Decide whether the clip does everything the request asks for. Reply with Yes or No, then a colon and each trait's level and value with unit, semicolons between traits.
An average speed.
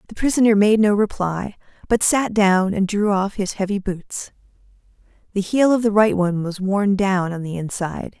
Yes: average, 190 wpm